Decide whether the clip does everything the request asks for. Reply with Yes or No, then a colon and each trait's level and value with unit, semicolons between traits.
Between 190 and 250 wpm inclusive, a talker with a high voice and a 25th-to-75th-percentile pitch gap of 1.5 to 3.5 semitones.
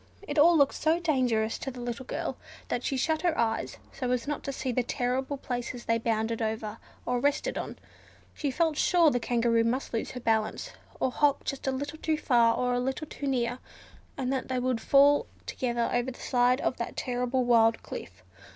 Yes: fast, 205 wpm; very high, 250 Hz; average, 2.8 semitones